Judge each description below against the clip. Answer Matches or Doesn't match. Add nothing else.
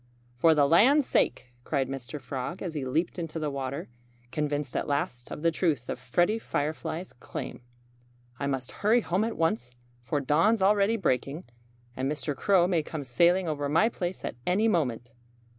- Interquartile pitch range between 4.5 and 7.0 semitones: Matches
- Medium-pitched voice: Matches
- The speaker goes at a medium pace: Matches